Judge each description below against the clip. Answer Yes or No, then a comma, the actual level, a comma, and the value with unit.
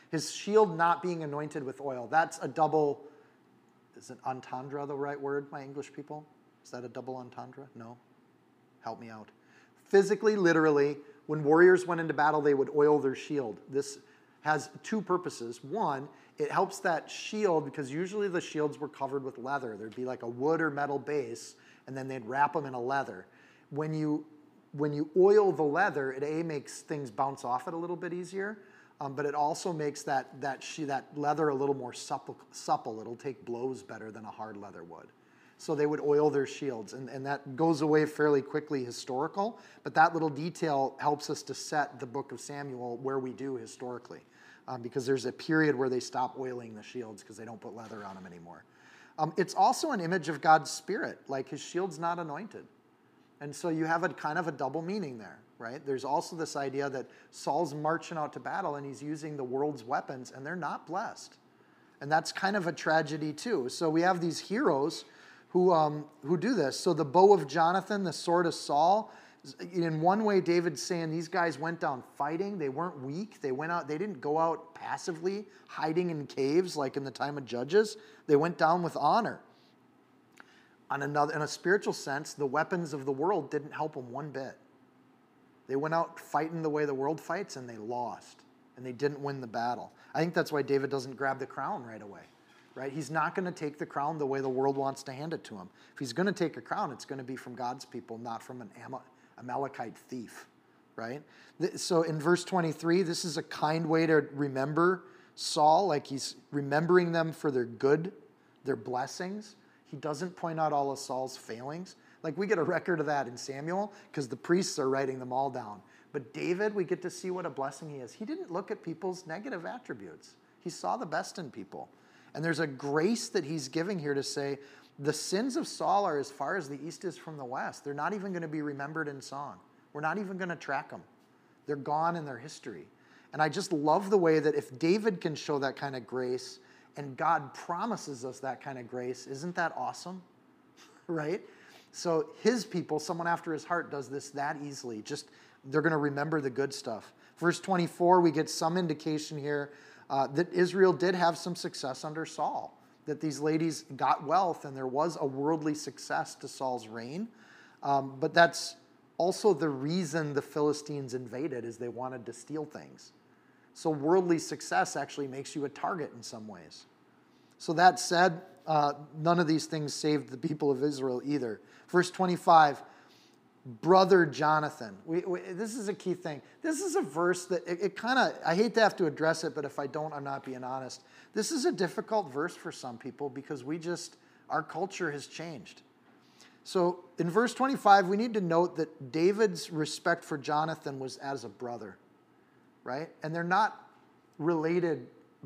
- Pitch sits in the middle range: Yes, medium, 150 Hz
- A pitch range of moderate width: Yes, average, 3.8 semitones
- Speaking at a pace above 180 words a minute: Yes, average, 200 wpm